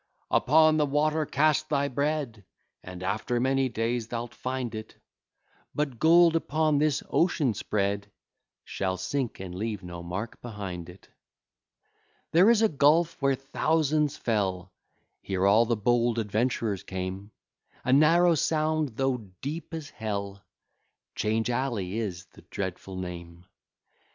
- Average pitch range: No, wide, 7.0 semitones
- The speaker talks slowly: Yes, slow, 130 wpm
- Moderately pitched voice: No, low, 120 Hz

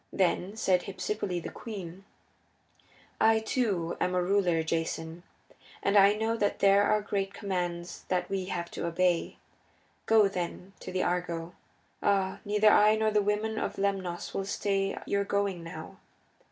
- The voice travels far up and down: No, narrow, 2.6 semitones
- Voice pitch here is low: No, high, 195 Hz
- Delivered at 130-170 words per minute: Yes, average, 155 wpm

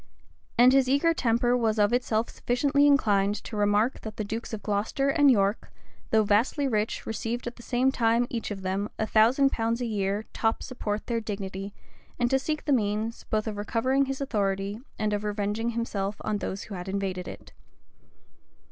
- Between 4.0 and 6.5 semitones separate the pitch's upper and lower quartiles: No, average, 3.1 semitones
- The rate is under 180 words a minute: No, average, 185 wpm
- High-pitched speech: Yes, high, 225 Hz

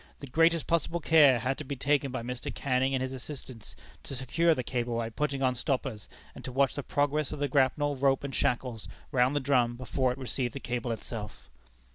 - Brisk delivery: Yes, fast, 210 wpm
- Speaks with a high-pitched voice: No, low, 130 Hz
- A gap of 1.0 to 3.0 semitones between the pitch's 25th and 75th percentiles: Yes, narrow, 2.4 semitones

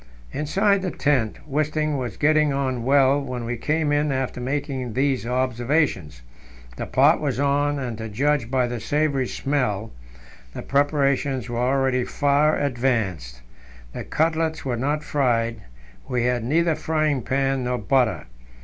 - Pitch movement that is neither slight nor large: Yes, average, 3.2 semitones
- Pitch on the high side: No, low, 135 Hz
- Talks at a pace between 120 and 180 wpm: Yes, average, 145 wpm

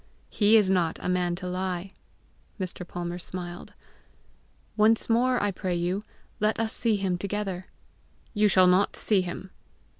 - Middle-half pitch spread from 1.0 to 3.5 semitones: Yes, average, 2.7 semitones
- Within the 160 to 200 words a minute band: No, average, 150 wpm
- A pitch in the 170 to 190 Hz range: Yes, medium, 185 Hz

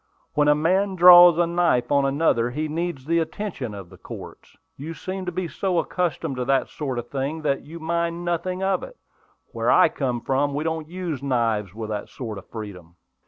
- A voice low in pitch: No, medium, 155 Hz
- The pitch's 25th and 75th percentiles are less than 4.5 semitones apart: No, wide, 5.4 semitones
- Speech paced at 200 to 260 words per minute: Yes, fast, 205 wpm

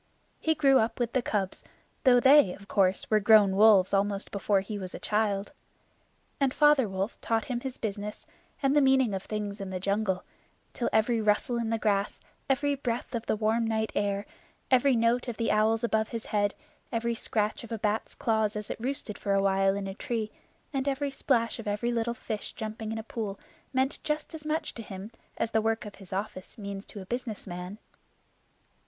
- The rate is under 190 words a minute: No, fast, 205 wpm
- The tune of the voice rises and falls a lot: No, average, 3.0 semitones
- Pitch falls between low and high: No, high, 220 Hz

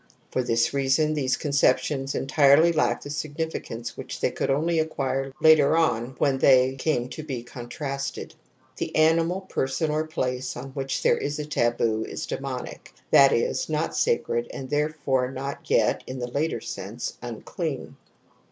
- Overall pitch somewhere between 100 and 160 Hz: Yes, medium, 140 Hz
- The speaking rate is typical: Yes, average, 160 wpm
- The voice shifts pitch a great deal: No, average, 3.1 semitones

